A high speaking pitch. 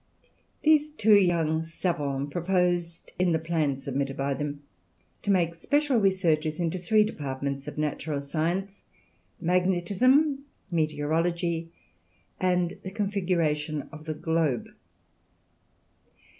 No: medium, 170 Hz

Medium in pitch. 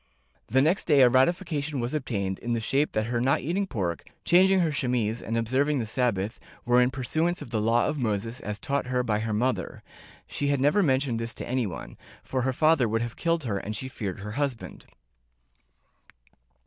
No: low, 125 Hz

